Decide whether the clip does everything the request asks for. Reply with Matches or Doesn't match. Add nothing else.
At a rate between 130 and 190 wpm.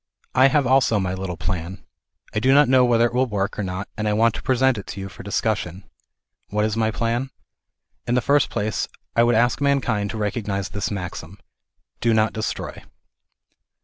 Doesn't match